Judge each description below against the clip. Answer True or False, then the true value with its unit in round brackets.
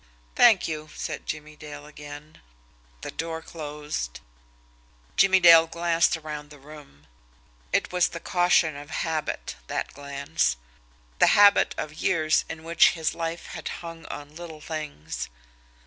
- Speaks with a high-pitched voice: False (155 Hz)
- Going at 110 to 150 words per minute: True (135 wpm)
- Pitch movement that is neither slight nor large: False (2.1 semitones)